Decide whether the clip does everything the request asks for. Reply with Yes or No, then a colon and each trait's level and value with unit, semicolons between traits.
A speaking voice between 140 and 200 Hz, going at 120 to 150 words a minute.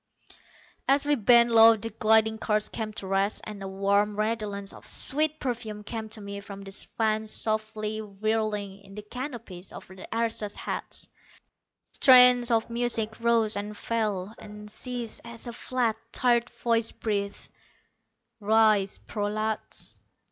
No: high, 220 Hz; average, 140 wpm